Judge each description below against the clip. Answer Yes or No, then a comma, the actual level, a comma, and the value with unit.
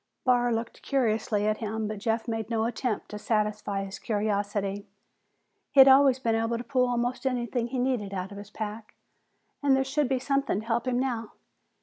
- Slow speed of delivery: No, average, 190 wpm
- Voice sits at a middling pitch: No, high, 230 Hz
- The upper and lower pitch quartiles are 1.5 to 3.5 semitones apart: Yes, average, 3.1 semitones